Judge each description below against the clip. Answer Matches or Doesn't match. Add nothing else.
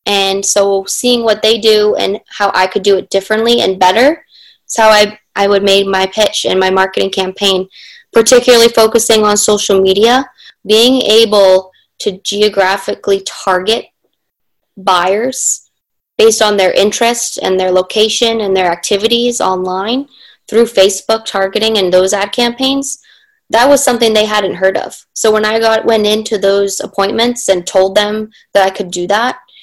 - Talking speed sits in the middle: Matches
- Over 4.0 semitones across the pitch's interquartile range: Doesn't match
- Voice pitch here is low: Doesn't match